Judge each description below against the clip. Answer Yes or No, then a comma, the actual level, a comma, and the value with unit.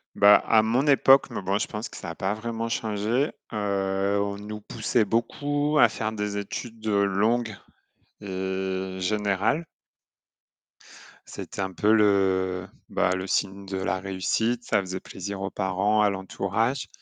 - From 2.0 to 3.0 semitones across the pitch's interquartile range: Yes, average, 2.7 semitones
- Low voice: Yes, low, 100 Hz